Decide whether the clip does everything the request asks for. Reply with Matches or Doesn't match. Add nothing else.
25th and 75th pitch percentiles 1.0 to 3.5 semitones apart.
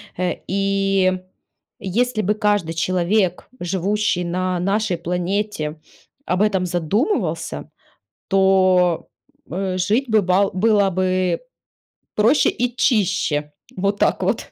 Matches